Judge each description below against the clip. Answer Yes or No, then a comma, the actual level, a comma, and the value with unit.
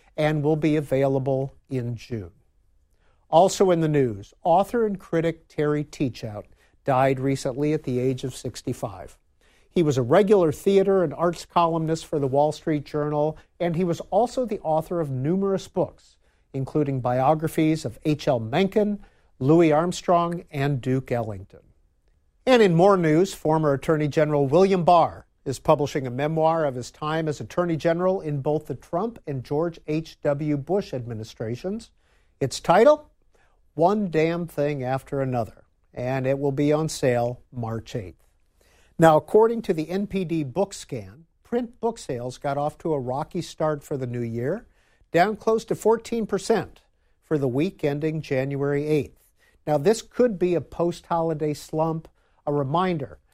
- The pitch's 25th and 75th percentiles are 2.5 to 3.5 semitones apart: No, average, 4.6 semitones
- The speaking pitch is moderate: Yes, medium, 150 Hz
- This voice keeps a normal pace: Yes, average, 155 wpm